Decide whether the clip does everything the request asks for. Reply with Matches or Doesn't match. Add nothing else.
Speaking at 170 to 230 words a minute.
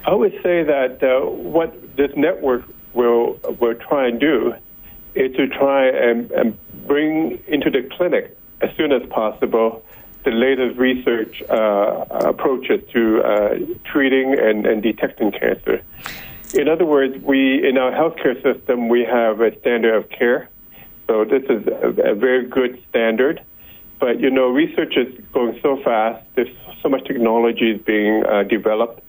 Doesn't match